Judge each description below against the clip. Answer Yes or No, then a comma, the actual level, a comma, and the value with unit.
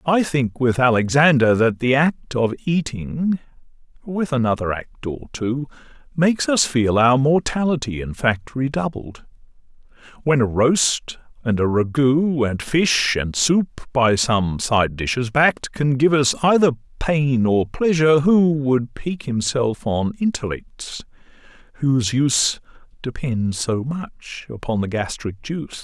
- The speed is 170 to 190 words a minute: No, slow, 135 wpm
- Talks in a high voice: No, low, 135 Hz